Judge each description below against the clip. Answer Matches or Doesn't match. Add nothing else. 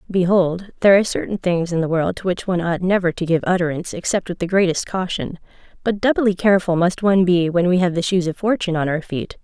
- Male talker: Doesn't match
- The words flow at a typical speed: Doesn't match